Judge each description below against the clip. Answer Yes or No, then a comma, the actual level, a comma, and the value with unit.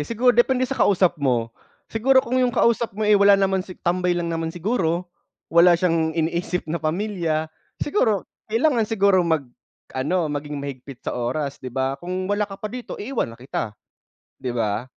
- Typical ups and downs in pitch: No, wide, 6.1 semitones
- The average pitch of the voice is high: No, medium, 175 Hz